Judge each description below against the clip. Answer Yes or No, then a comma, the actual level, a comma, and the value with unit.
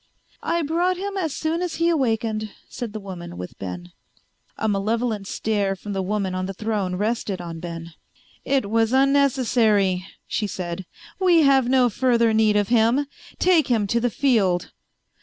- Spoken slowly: No, average, 165 wpm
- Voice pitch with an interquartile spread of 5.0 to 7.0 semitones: Yes, wide, 5.5 semitones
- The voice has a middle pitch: No, high, 220 Hz